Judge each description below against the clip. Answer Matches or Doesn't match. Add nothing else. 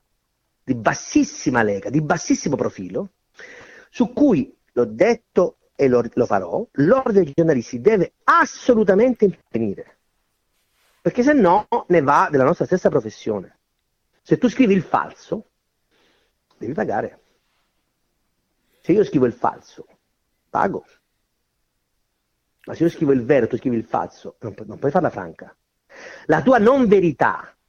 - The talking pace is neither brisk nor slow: Matches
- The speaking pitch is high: Doesn't match